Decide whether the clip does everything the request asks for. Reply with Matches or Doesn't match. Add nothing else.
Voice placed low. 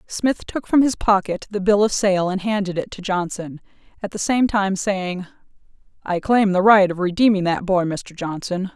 Doesn't match